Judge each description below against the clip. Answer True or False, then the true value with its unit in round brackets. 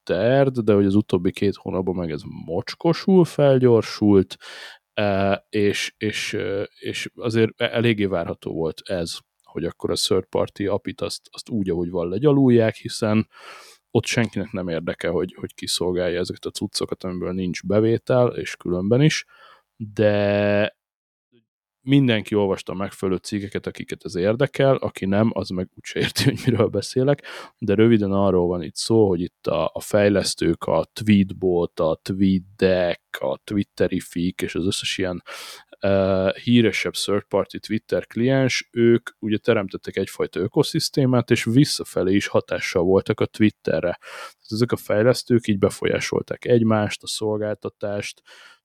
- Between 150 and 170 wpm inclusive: False (140 wpm)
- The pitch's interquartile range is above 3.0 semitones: True (3.6 semitones)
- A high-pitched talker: False (105 Hz)